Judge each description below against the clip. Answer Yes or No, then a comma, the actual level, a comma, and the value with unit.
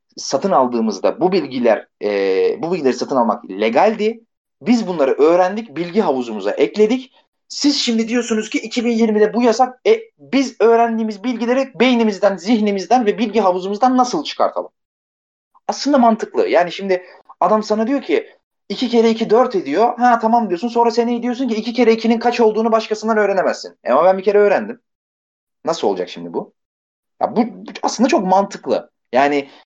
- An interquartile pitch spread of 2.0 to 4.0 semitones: Yes, average, 3.1 semitones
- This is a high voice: Yes, high, 230 Hz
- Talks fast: Yes, fast, 155 wpm